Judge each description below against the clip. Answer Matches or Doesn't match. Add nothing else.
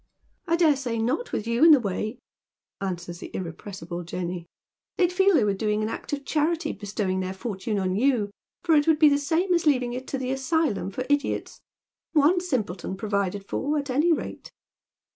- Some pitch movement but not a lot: Doesn't match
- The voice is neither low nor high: Doesn't match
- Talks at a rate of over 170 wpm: Matches